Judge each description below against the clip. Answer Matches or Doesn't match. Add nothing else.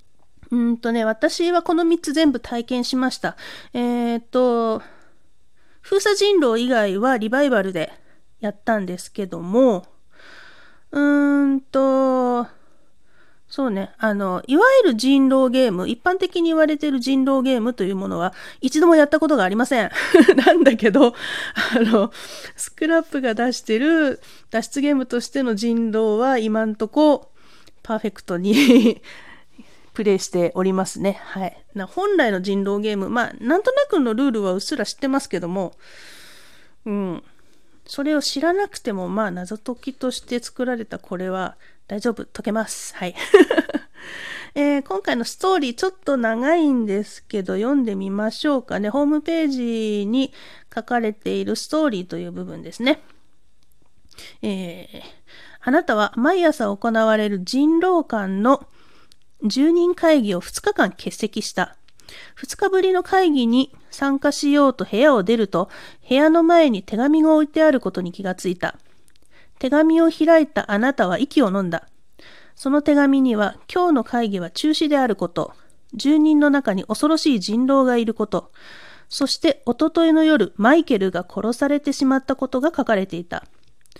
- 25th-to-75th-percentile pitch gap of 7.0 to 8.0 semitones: Doesn't match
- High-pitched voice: Matches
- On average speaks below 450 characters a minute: Matches